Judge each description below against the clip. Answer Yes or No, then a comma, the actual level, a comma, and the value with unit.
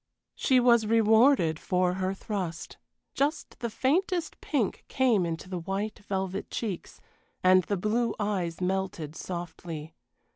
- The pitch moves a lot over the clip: No, average, 4.3 semitones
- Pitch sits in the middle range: No, high, 195 Hz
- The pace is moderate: No, slow, 130 wpm